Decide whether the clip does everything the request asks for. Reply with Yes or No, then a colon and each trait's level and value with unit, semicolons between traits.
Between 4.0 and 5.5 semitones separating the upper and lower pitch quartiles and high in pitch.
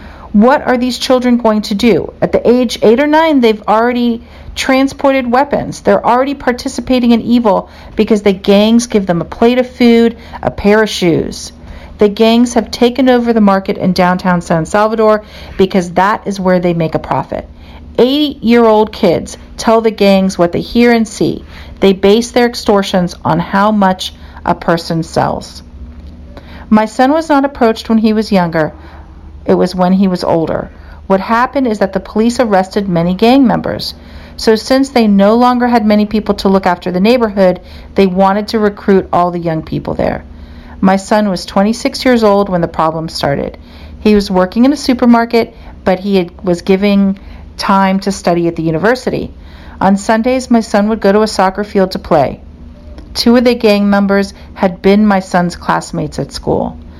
Yes: average, 4.4 semitones; high, 205 Hz